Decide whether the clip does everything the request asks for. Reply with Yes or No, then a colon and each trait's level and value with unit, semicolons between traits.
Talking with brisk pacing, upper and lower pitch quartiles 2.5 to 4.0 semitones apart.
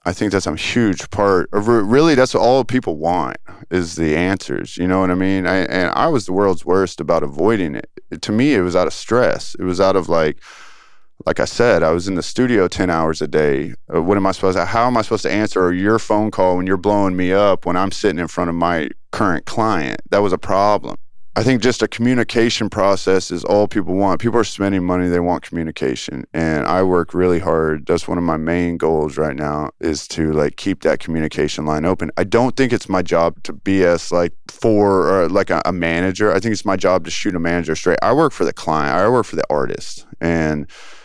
Yes: fast, 235 wpm; average, 3.2 semitones